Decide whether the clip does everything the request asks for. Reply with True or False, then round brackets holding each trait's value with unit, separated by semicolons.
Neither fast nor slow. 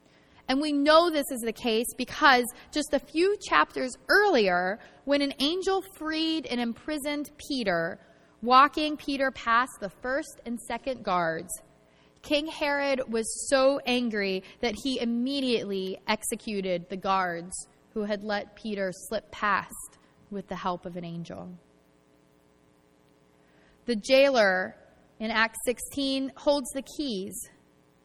False (125 wpm)